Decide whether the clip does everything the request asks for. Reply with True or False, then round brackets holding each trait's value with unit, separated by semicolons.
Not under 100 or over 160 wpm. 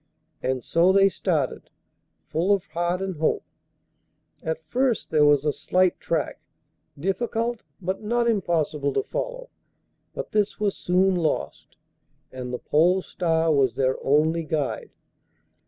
True (135 wpm)